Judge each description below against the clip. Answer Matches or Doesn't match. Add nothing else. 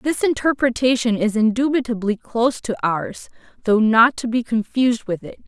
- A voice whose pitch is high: Matches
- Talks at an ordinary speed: Matches